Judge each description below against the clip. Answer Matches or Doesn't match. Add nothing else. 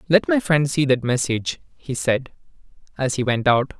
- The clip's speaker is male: Matches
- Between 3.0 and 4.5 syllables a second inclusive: Doesn't match